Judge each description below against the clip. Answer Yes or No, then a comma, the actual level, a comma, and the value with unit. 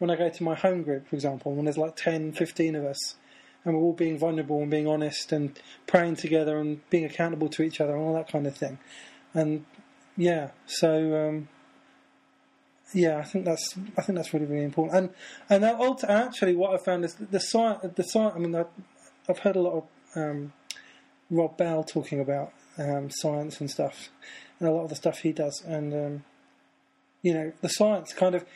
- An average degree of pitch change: Yes, average, 3.3 semitones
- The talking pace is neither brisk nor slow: No, fast, 210 wpm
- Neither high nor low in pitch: Yes, medium, 160 Hz